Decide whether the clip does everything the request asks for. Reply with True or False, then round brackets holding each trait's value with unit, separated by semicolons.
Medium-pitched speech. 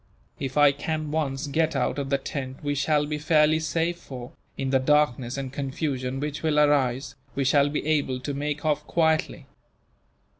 True (145 Hz)